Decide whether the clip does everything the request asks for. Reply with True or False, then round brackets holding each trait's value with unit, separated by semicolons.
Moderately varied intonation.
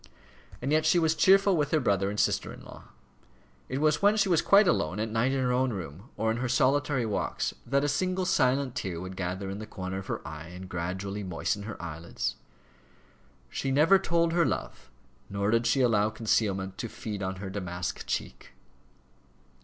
False (7.3 semitones)